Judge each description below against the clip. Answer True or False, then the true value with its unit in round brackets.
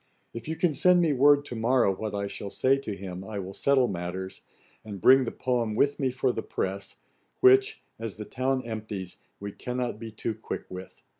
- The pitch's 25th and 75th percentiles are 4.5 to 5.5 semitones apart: True (5.1 semitones)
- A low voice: True (115 Hz)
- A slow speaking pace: False (205 wpm)